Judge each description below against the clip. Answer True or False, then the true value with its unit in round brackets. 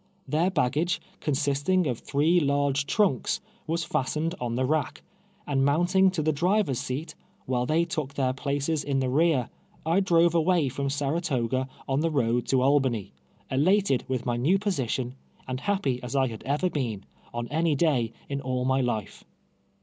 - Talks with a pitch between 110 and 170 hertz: True (140 Hz)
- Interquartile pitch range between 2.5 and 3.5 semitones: False (4.4 semitones)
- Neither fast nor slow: True (165 wpm)